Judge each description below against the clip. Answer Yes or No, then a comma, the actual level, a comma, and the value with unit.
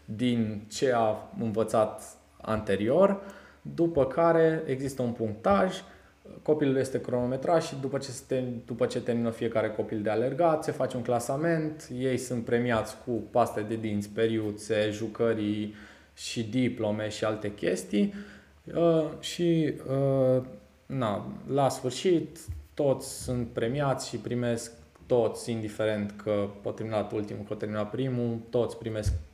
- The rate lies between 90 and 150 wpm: Yes, average, 120 wpm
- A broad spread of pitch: No, average, 3.7 semitones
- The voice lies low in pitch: Yes, low, 120 Hz